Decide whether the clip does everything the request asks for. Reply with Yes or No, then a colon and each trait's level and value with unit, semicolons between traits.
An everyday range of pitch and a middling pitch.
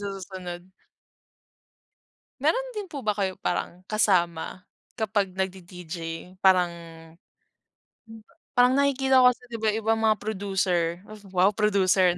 No: average, 3.3 semitones; high, 200 Hz